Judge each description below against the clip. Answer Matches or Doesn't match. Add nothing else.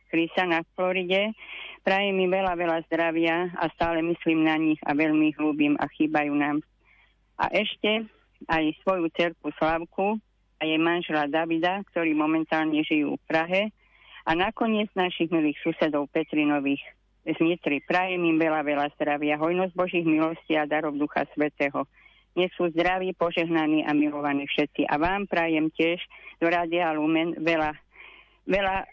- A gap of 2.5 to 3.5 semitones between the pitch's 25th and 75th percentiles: Matches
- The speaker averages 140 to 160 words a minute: Matches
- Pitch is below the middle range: Doesn't match